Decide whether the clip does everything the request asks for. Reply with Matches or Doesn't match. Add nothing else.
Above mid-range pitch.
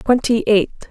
Matches